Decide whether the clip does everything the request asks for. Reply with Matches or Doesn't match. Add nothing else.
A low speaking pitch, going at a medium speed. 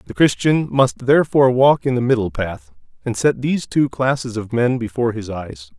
Matches